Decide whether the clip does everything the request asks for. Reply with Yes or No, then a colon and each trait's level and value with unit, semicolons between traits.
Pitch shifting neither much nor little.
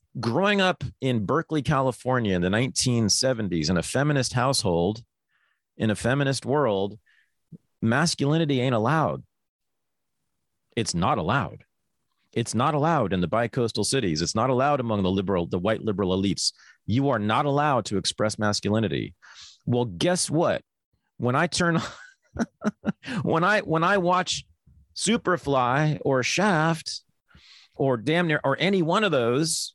No: wide, 6.7 semitones